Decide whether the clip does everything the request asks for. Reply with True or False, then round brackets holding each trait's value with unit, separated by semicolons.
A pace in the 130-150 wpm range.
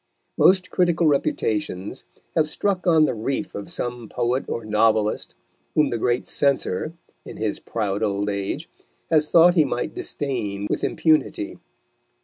True (140 wpm)